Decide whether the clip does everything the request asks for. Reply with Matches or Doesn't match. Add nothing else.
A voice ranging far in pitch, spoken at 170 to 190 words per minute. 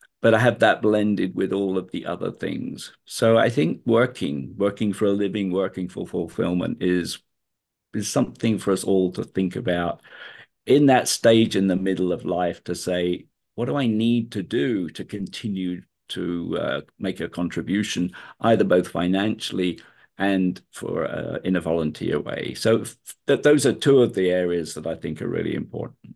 Doesn't match